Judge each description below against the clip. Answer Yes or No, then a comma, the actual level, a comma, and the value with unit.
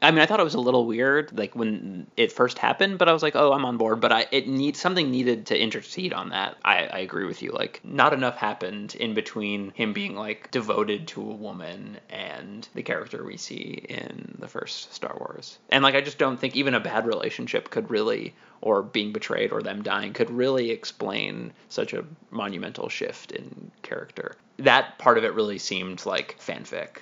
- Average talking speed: No, fast, 210 wpm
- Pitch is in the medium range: No, low, 130 Hz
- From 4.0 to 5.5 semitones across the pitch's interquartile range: Yes, average, 4.4 semitones